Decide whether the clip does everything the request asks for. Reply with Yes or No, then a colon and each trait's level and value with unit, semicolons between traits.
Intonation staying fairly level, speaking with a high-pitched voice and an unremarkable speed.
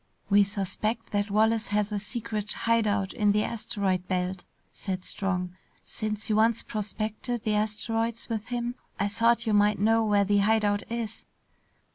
Yes: narrow, 1.9 semitones; high, 210 Hz; average, 165 wpm